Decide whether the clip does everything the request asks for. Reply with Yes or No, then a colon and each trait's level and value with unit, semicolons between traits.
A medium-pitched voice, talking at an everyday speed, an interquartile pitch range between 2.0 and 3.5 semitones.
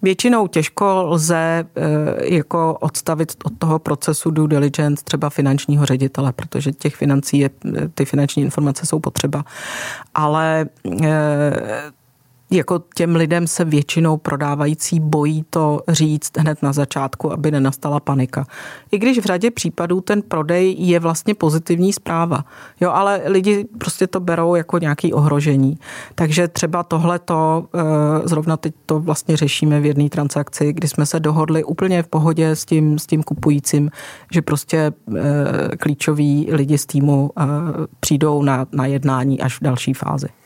Yes: medium, 155 Hz; average, 145 wpm; narrow, 2.4 semitones